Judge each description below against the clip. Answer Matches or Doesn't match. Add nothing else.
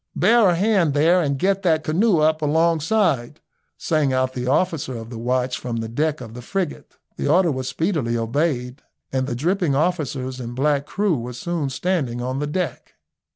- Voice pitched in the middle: Matches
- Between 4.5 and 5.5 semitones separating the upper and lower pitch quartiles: Matches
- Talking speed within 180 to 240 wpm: Matches